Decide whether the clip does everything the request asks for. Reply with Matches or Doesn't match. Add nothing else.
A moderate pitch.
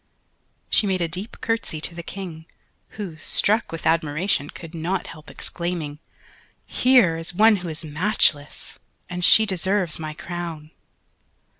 Matches